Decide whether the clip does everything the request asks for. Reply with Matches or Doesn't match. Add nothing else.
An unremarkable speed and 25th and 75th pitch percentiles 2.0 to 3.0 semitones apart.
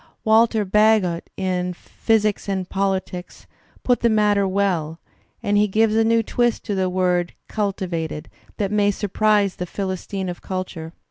Matches